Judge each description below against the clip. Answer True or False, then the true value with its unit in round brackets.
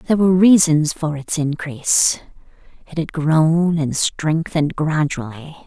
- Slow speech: True (125 wpm)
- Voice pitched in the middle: True (155 Hz)